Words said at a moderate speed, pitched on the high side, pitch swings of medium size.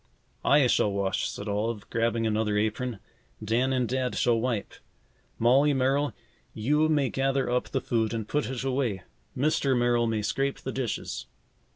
No: average, 160 wpm; low, 120 Hz; average, 3.2 semitones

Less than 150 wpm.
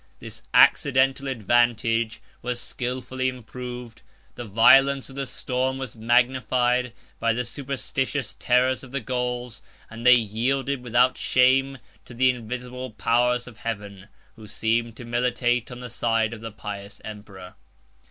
Yes: average, 140 wpm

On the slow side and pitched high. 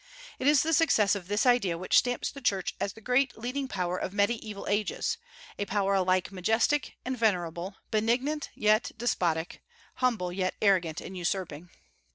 No: average, 165 wpm; high, 205 Hz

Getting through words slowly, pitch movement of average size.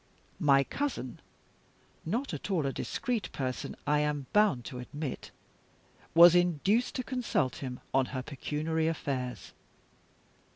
No: slow, 125 wpm; wide, 6.1 semitones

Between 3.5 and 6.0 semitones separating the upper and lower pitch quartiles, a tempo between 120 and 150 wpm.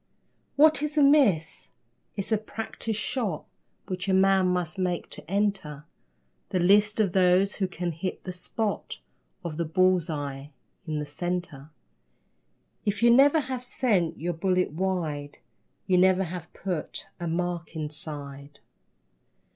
Yes: average, 4.1 semitones; average, 140 wpm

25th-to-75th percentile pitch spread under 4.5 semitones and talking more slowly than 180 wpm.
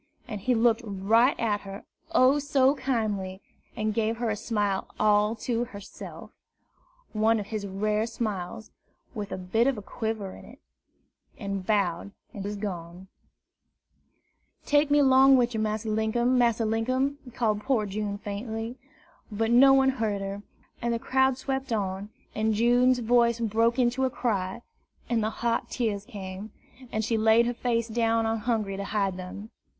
Yes: average, 2.8 semitones; average, 165 wpm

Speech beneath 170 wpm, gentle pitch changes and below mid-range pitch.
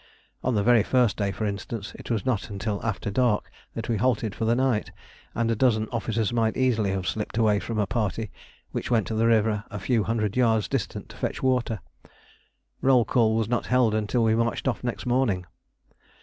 No: fast, 205 wpm; narrow, 2.3 semitones; low, 115 Hz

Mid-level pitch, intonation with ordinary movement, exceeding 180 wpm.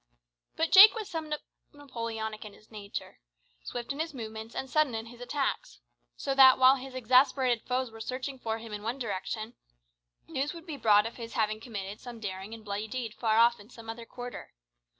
No: high, 235 Hz; average, 3.4 semitones; average, 195 wpm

